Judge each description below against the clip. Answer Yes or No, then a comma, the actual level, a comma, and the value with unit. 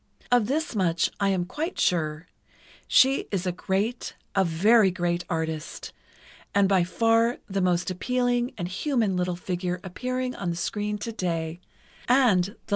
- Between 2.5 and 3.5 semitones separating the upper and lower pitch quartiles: No, average, 4.9 semitones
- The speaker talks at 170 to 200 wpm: No, average, 150 wpm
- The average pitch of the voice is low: No, high, 190 Hz